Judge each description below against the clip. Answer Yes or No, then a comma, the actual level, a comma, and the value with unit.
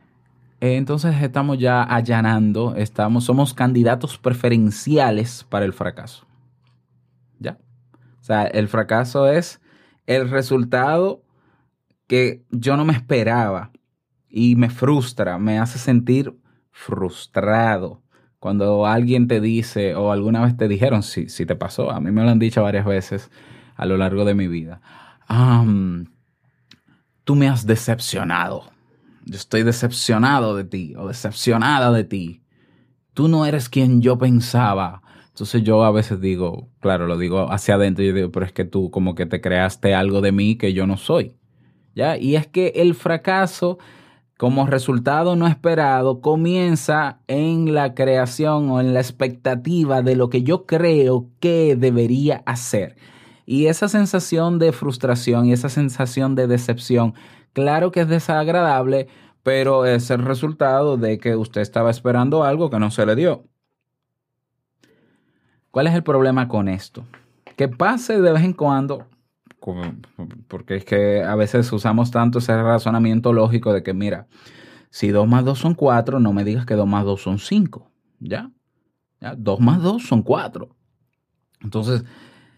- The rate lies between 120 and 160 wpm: Yes, average, 150 wpm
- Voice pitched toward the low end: Yes, low, 125 Hz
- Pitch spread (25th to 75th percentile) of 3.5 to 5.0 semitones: Yes, average, 4.3 semitones